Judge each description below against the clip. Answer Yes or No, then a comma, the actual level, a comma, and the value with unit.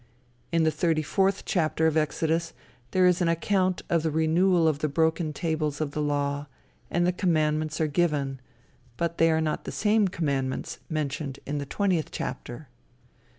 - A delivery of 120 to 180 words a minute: Yes, average, 170 wpm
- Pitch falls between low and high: Yes, medium, 160 Hz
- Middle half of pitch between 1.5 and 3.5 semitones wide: Yes, narrow, 2.4 semitones